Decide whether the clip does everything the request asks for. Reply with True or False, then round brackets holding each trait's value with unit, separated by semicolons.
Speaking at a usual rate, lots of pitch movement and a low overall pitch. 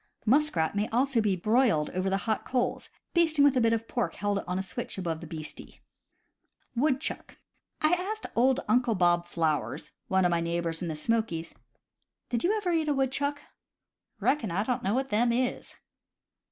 False (185 wpm; 7.0 semitones; 225 Hz)